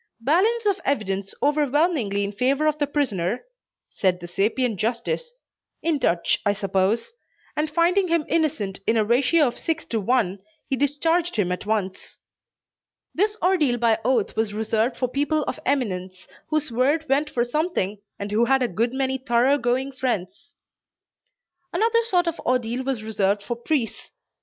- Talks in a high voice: Yes, very high, 250 Hz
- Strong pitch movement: Yes, wide, 6.1 semitones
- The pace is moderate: Yes, average, 160 wpm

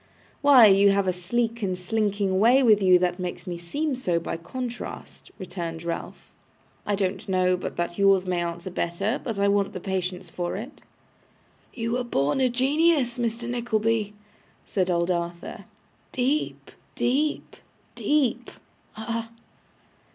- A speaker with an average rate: Yes, average, 145 wpm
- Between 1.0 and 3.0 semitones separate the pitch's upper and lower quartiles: No, average, 4.8 semitones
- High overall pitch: Yes, high, 200 Hz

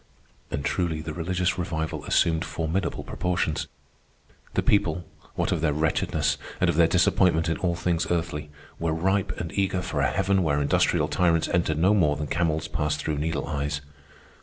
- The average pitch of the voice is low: Yes, very low, 80 Hz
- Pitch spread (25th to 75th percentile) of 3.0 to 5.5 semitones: No, narrow, 2.5 semitones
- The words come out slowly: No, average, 170 wpm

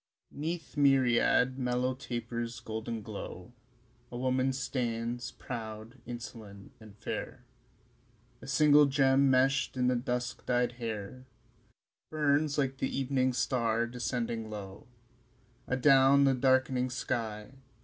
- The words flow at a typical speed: No, slow, 115 wpm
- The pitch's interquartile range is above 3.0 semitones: No, narrow, 2.4 semitones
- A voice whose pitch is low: Yes, low, 125 Hz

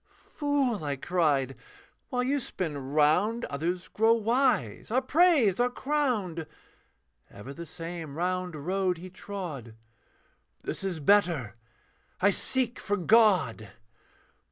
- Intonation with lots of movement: Yes, wide, 6.8 semitones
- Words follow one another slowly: Yes, slow, 115 wpm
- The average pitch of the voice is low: No, medium, 185 Hz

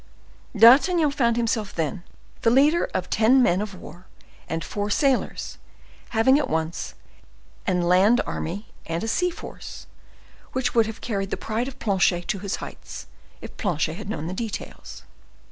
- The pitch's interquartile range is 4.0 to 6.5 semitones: Yes, average, 5.1 semitones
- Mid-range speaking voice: No, high, 215 Hz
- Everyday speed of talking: Yes, average, 160 wpm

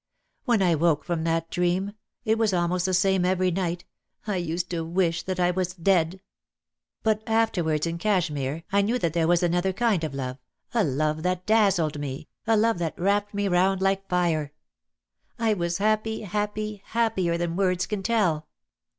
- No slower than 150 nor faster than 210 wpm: Yes, average, 185 wpm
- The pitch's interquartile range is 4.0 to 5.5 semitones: No, average, 3.4 semitones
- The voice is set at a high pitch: No, medium, 180 Hz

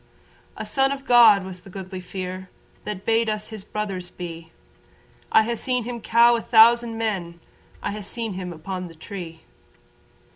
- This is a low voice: No, high, 205 Hz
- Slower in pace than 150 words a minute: No, average, 170 wpm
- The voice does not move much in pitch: No, average, 3.9 semitones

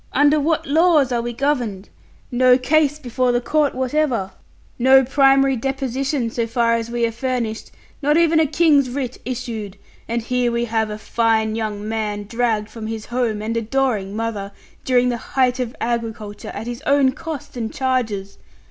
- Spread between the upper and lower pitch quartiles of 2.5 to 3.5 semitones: Yes, average, 3.2 semitones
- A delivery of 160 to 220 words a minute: Yes, average, 170 wpm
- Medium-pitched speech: No, high, 245 Hz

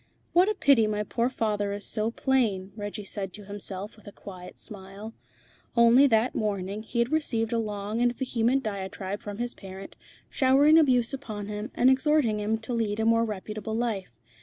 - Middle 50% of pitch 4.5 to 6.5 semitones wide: No, average, 3.0 semitones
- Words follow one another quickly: No, average, 185 wpm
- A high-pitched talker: Yes, high, 220 Hz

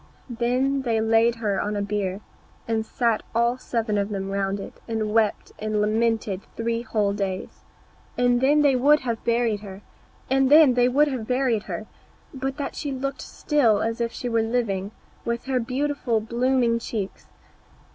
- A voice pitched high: Yes, high, 230 Hz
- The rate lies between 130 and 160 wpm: Yes, average, 145 wpm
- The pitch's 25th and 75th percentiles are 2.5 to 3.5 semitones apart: Yes, average, 3.2 semitones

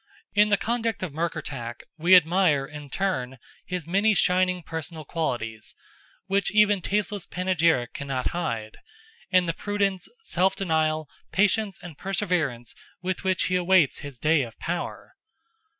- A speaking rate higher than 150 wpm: No, slow, 135 wpm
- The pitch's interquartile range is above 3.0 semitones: Yes, average, 4.5 semitones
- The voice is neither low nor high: Yes, medium, 175 Hz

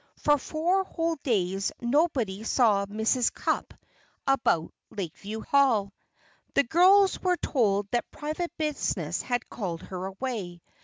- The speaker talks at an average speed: No, slow, 120 wpm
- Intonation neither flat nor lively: No, wide, 7.4 semitones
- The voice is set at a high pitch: Yes, high, 240 Hz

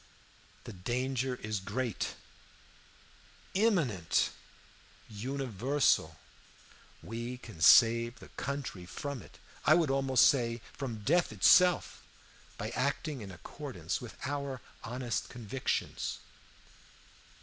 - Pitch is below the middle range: Yes, low, 125 Hz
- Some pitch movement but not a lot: Yes, average, 4.2 semitones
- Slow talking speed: Yes, slow, 95 wpm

